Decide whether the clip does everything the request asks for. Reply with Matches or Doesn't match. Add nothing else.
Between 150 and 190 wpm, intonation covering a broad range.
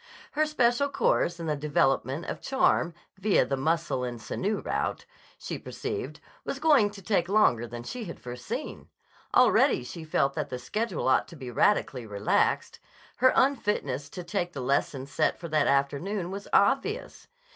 Matches